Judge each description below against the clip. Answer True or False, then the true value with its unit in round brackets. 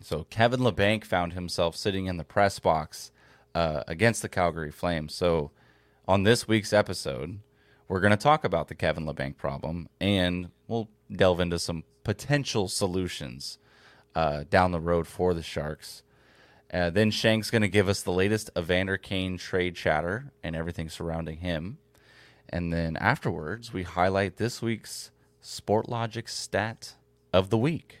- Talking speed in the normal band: True (155 wpm)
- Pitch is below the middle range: True (95 Hz)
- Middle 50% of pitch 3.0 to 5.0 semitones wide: True (4.3 semitones)